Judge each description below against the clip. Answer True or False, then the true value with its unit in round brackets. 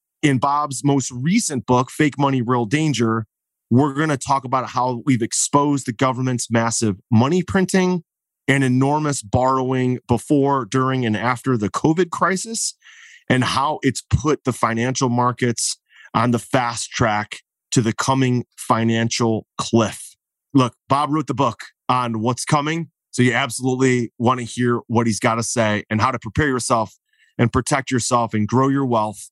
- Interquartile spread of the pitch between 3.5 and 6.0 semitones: False (2.9 semitones)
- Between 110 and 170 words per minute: True (160 wpm)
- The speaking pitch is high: False (125 Hz)